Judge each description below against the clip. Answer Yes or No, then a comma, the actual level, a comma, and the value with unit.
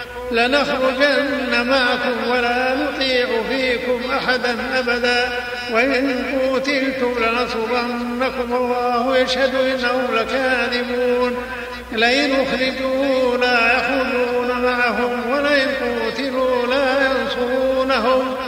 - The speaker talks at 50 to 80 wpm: Yes, average, 75 wpm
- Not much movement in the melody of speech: Yes, narrow, 1.2 semitones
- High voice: Yes, very high, 250 Hz